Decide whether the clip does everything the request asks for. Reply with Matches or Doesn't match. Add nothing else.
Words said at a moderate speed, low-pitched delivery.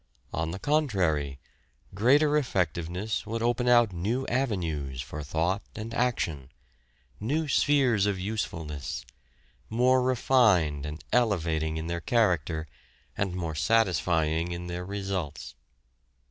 Doesn't match